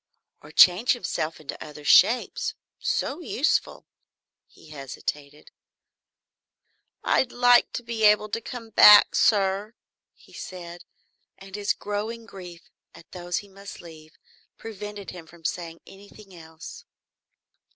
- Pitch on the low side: No, high, 195 Hz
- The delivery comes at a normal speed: No, slow, 120 wpm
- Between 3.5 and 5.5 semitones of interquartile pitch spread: Yes, average, 4.4 semitones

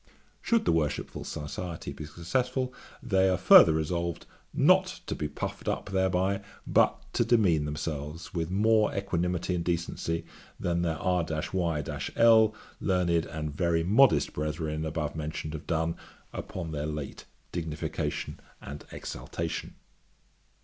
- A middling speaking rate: No, slow, 130 wpm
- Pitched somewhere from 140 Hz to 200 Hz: No, very low, 85 Hz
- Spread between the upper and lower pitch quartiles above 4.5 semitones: No, average, 3.3 semitones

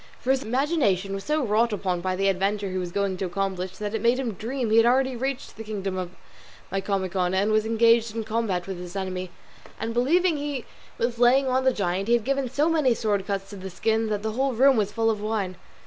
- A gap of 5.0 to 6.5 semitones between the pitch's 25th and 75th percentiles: No, average, 4.2 semitones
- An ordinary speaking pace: No, fast, 235 wpm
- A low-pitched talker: No, high, 215 Hz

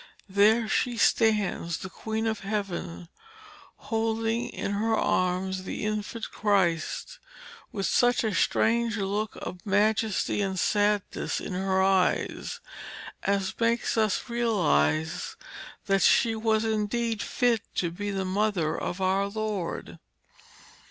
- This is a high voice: Yes, high, 205 Hz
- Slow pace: Yes, slow, 120 wpm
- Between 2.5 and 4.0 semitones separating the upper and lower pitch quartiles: Yes, average, 2.8 semitones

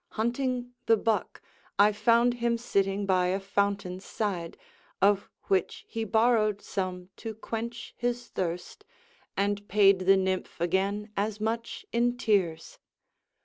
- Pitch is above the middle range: Yes, high, 205 Hz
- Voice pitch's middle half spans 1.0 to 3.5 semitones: Yes, average, 3.2 semitones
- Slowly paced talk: Yes, slow, 130 wpm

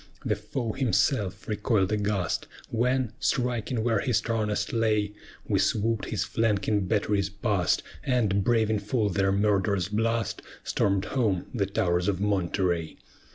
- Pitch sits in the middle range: No, low, 105 Hz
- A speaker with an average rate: No, slow, 130 wpm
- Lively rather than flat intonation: No, narrow, 2.5 semitones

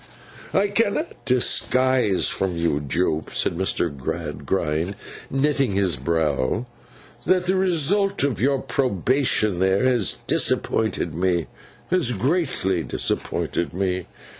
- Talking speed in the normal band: No, slow, 110 wpm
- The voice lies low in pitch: Yes, low, 100 Hz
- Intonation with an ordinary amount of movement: No, wide, 8.3 semitones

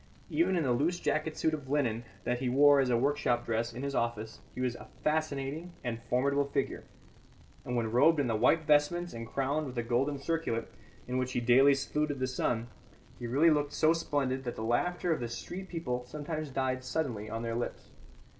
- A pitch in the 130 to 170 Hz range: Yes, low, 135 Hz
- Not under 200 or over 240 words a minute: Yes, fast, 205 wpm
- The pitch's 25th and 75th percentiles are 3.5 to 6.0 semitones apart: Yes, average, 4.0 semitones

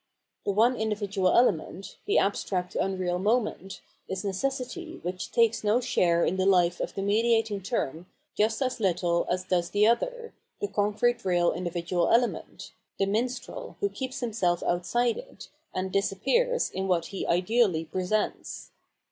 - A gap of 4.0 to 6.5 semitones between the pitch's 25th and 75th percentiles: Yes, average, 4.5 semitones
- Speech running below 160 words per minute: Yes, average, 150 wpm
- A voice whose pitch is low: No, high, 200 Hz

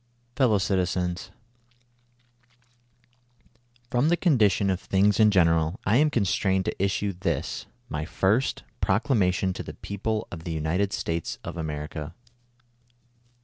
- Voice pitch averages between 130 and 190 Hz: No, low, 100 Hz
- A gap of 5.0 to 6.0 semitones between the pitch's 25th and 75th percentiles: Yes, wide, 5.4 semitones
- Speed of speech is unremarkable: No, slow, 130 wpm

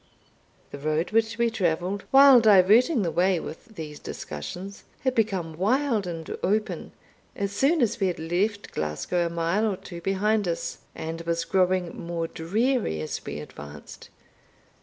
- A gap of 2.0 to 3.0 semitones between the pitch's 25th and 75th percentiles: No, average, 4.7 semitones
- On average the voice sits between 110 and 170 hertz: No, medium, 185 Hz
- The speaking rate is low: No, average, 155 wpm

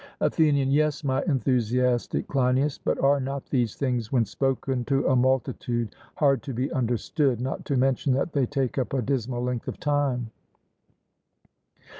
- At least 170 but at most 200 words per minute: No, average, 155 wpm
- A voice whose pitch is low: Yes, low, 130 Hz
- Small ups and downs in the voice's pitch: Yes, narrow, 2.0 semitones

